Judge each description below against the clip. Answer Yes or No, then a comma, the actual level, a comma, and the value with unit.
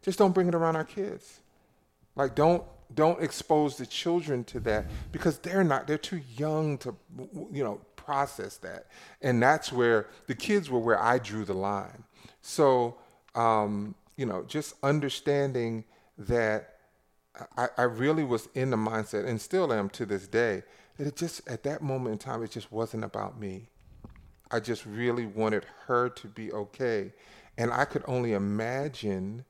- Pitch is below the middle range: Yes, low, 120 Hz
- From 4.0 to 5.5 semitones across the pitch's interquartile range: Yes, average, 5.2 semitones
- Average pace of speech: Yes, average, 170 wpm